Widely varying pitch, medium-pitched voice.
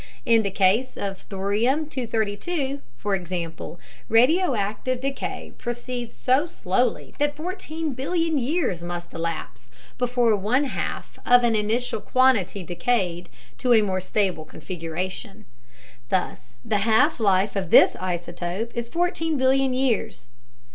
No: wide, 5.8 semitones; high, 225 Hz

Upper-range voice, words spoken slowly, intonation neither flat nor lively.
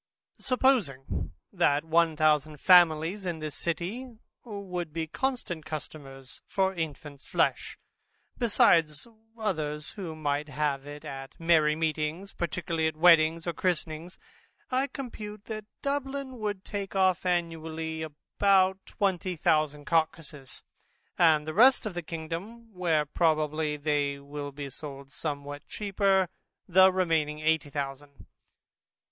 No: medium, 160 Hz; slow, 120 wpm; average, 4.0 semitones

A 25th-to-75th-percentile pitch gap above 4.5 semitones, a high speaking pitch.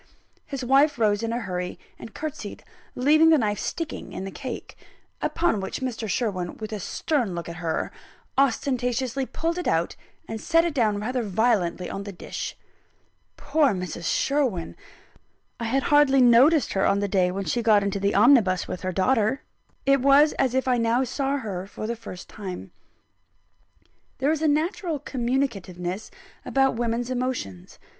Yes: wide, 5.5 semitones; high, 235 Hz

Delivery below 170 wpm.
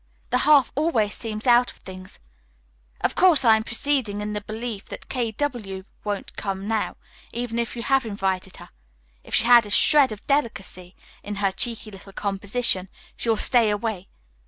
No: average, 180 wpm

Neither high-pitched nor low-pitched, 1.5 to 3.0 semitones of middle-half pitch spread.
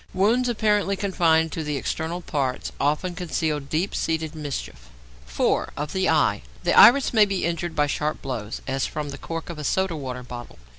No: medium, 160 Hz; average, 4.5 semitones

